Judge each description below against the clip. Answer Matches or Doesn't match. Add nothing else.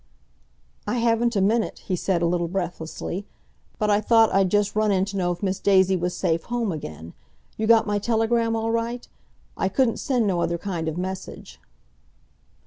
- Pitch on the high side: Matches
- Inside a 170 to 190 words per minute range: Matches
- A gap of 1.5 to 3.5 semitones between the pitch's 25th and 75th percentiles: Doesn't match